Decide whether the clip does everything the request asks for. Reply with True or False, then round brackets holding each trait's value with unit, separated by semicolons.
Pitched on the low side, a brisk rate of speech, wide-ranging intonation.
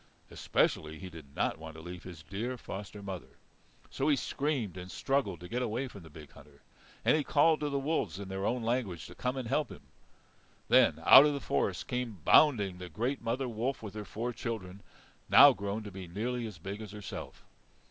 True (105 Hz; 210 wpm; 5.7 semitones)